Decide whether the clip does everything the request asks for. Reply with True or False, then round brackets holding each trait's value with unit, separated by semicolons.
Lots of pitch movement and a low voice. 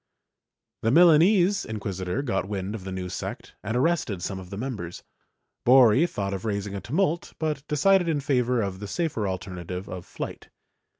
True (7.8 semitones; 110 Hz)